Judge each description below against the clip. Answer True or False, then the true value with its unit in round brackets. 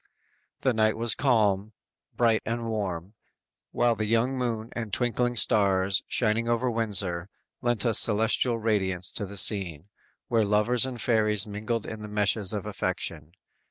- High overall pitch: False (110 Hz)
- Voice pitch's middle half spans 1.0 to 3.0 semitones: True (2.6 semitones)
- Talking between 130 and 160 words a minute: True (150 wpm)